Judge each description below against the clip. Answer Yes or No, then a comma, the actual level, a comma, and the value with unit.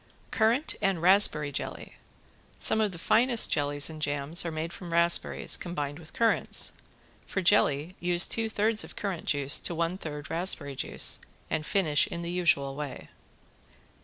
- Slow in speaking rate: No, average, 160 wpm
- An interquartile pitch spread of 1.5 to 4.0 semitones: No, average, 4.7 semitones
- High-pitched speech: No, medium, 170 Hz